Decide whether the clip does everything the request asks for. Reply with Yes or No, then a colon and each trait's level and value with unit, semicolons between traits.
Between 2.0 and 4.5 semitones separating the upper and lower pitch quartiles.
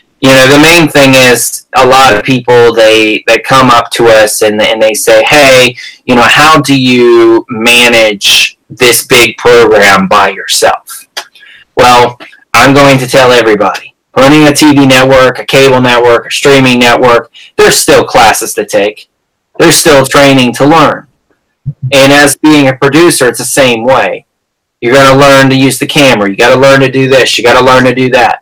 Yes: average, 2.8 semitones